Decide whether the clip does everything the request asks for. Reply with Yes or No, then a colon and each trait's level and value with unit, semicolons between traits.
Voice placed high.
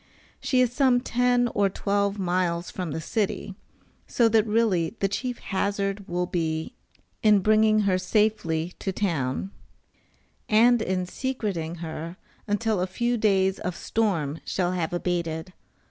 Yes: high, 195 Hz